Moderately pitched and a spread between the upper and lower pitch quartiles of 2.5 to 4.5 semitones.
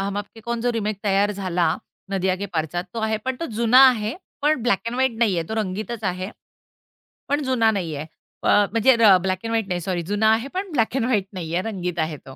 No: high, 205 Hz; average, 4.1 semitones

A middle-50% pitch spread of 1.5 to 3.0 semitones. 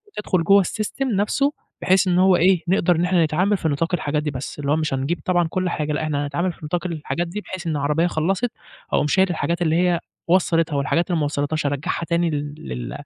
No: average, 3.5 semitones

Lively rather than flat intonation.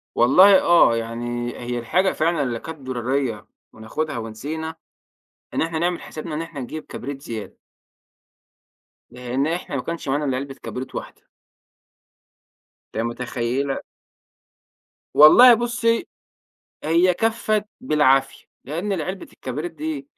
Yes: wide, 5.8 semitones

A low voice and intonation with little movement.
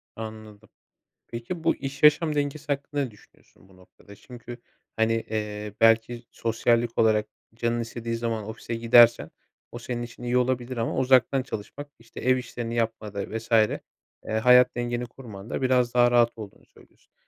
Yes: low, 115 Hz; narrow, 2.0 semitones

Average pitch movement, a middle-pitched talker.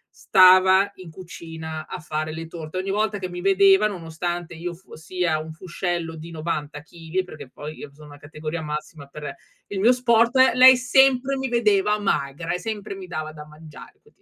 Yes: average, 4.0 semitones; medium, 175 Hz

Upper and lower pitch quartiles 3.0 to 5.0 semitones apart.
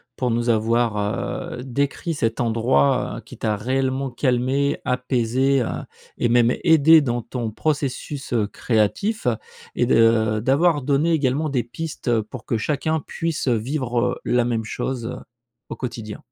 Yes: average, 3.4 semitones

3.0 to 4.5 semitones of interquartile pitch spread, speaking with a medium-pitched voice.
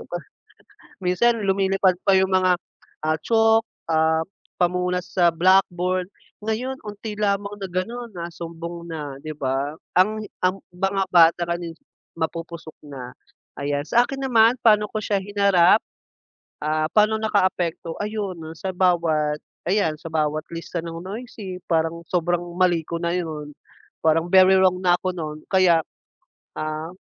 Yes: average, 3.3 semitones; medium, 180 Hz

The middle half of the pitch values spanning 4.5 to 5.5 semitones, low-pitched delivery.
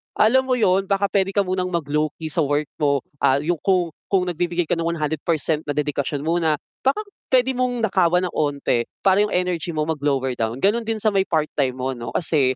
No: average, 4.8 semitones; medium, 170 Hz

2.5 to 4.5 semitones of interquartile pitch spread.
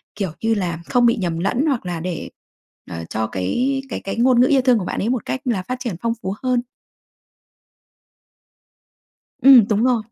No: wide, 5.5 semitones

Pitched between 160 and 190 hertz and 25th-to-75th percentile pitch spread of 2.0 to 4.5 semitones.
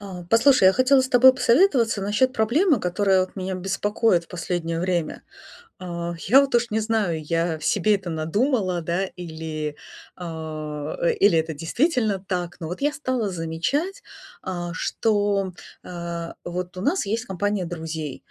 No: medium, 185 Hz; average, 5.0 semitones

